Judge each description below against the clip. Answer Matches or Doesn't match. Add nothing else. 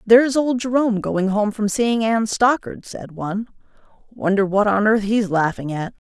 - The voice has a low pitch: Doesn't match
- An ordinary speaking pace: Matches